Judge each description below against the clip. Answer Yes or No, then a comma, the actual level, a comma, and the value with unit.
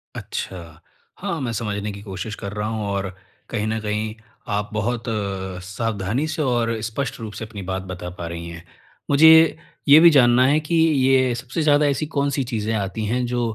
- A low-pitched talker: Yes, low, 110 Hz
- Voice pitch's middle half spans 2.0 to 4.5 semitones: No, average, 4.9 semitones